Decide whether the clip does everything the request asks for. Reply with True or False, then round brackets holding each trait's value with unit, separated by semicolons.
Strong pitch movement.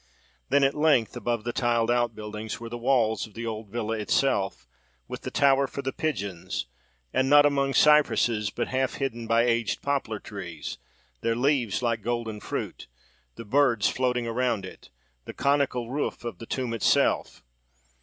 False (3.4 semitones)